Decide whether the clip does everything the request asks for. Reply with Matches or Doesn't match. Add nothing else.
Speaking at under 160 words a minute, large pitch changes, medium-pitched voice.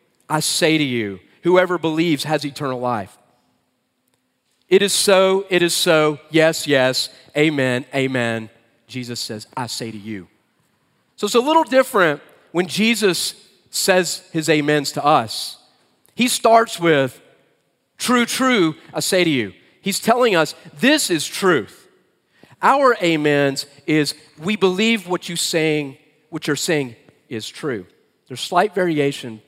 Matches